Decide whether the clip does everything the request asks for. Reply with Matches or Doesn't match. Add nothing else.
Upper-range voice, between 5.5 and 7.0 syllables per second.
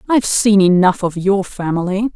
Doesn't match